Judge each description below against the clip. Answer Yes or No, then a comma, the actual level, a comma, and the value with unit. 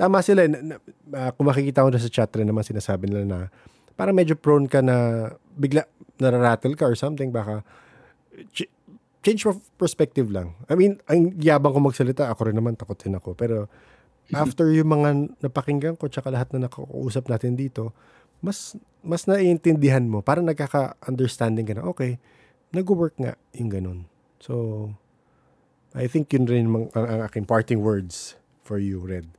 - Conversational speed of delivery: Yes, average, 165 wpm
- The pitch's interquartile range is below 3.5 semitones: No, average, 5.3 semitones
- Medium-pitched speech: No, low, 130 Hz